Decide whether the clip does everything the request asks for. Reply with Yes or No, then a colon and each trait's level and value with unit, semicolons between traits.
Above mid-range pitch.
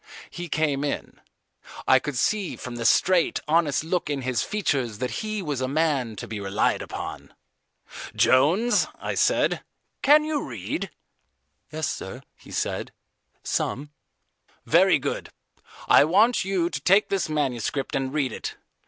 No: medium, 150 Hz